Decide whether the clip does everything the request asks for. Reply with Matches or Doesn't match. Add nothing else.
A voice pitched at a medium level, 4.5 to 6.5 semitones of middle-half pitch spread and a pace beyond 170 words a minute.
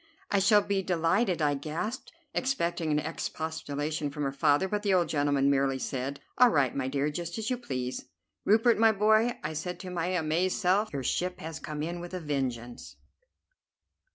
Matches